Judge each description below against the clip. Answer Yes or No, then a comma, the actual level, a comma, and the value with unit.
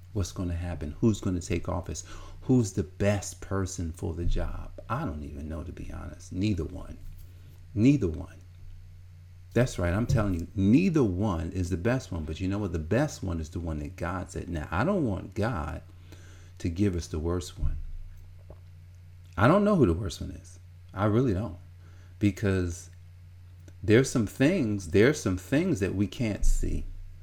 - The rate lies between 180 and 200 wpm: Yes, average, 185 wpm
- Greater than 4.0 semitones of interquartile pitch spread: No, narrow, 2.4 semitones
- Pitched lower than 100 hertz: Yes, very low, 90 Hz